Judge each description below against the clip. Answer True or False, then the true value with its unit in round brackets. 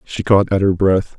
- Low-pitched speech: True (95 Hz)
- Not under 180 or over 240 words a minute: False (250 wpm)